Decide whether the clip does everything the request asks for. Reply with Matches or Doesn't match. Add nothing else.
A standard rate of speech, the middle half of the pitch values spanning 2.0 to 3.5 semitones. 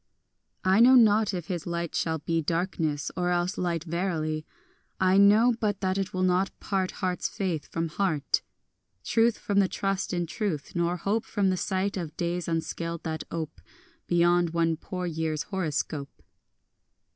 Matches